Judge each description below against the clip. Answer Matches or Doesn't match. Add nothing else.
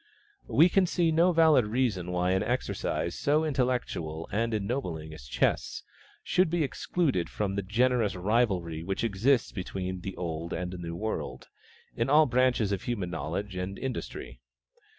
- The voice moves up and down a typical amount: Doesn't match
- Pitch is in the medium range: Doesn't match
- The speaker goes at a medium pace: Matches